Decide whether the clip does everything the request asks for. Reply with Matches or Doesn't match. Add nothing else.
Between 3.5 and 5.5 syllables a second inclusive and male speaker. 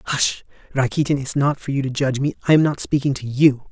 Doesn't match